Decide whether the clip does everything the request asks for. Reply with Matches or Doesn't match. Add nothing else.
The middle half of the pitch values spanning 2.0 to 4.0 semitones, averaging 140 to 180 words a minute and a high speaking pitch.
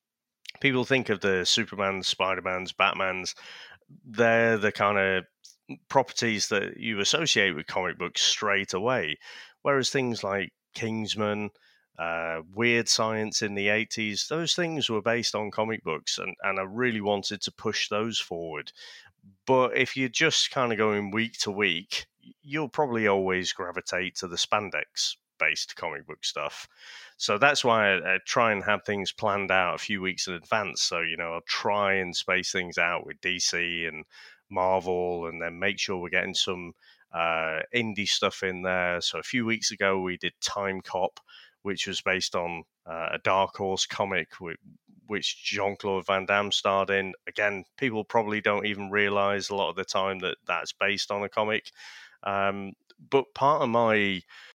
Doesn't match